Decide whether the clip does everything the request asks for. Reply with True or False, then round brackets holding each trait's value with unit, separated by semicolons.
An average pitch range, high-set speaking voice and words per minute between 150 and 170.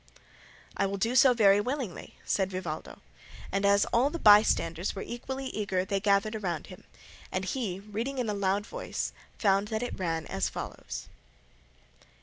True (3.3 semitones; 200 Hz; 160 wpm)